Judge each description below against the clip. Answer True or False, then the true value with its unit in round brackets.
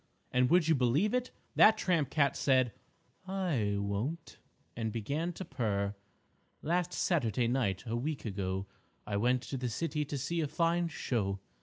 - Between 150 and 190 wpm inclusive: True (160 wpm)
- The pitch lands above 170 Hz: False (135 Hz)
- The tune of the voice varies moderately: False (6.9 semitones)